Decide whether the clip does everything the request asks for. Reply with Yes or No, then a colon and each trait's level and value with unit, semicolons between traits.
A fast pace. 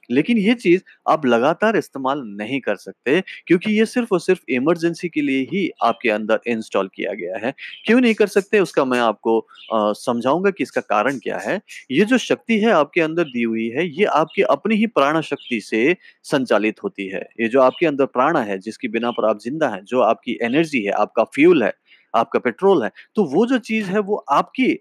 Yes: fast, 205 wpm